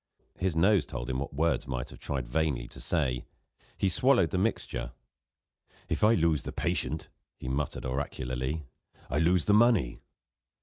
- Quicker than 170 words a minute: No, average, 160 wpm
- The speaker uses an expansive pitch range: Yes, wide, 6.1 semitones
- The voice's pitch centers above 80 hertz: No, very low, 75 Hz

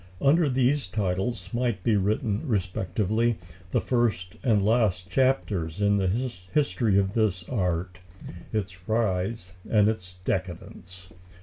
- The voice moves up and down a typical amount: Yes, average, 4.3 semitones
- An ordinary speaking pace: No, slow, 120 wpm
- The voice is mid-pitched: No, low, 100 Hz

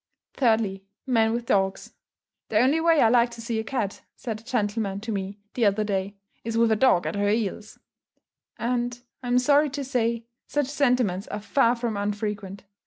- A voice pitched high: Yes, high, 225 Hz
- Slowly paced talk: No, average, 180 wpm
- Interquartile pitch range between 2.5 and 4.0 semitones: Yes, average, 3.2 semitones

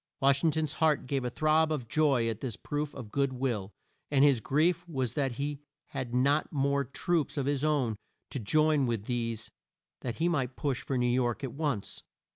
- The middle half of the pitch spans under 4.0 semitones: Yes, average, 3.4 semitones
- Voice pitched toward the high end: No, medium, 140 Hz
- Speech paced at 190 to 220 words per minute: Yes, average, 200 wpm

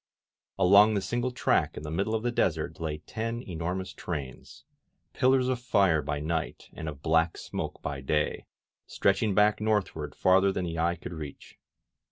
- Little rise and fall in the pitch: No, wide, 5.4 semitones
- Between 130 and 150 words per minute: No, average, 175 wpm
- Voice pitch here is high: No, very low, 90 Hz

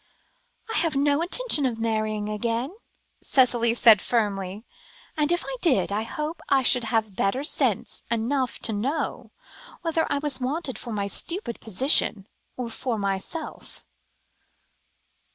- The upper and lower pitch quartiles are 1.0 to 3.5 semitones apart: No, average, 5.2 semitones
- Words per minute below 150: Yes, slow, 135 wpm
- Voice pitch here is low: No, high, 240 Hz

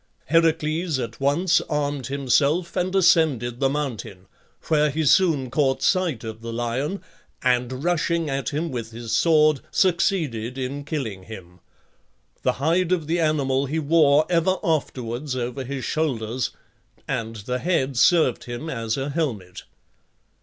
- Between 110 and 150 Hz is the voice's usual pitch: Yes, medium, 140 Hz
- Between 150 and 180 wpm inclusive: No, average, 140 wpm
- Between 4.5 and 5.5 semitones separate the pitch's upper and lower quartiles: Yes, average, 4.8 semitones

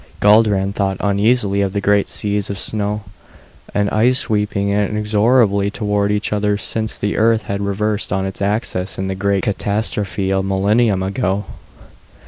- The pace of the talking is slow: No, average, 150 wpm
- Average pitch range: No, narrow, 1.3 semitones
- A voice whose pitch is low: Yes, low, 100 Hz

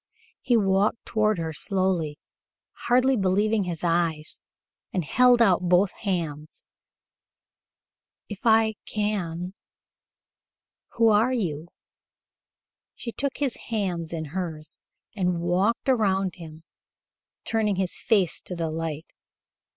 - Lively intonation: No, average, 4.5 semitones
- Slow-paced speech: Yes, slow, 110 wpm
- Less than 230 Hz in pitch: Yes, high, 190 Hz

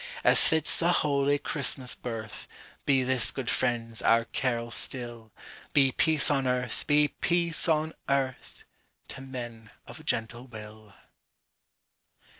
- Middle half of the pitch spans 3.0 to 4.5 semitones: Yes, average, 3.6 semitones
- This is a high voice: No, low, 130 Hz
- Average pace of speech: No, slow, 110 wpm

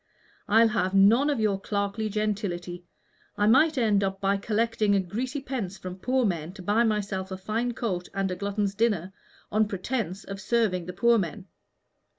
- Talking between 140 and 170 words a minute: Yes, average, 165 wpm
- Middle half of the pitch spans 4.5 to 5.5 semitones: No, average, 3.1 semitones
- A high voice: Yes, high, 205 Hz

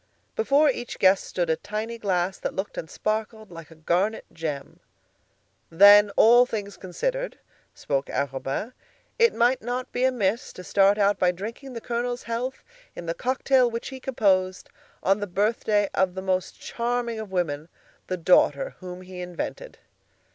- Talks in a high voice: Yes, high, 205 Hz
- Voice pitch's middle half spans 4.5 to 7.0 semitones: Yes, average, 4.9 semitones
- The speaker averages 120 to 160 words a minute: Yes, average, 155 wpm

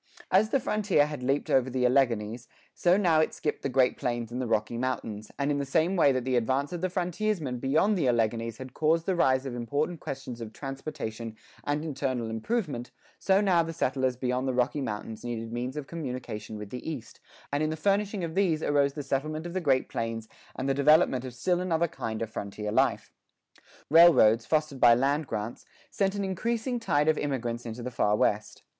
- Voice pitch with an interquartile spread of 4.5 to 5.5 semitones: Yes, average, 5.1 semitones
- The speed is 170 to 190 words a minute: No, fast, 205 wpm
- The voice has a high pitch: No, low, 135 Hz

